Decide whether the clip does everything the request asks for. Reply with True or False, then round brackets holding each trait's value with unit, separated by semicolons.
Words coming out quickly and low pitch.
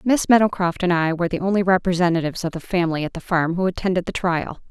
False (230 wpm; 180 Hz)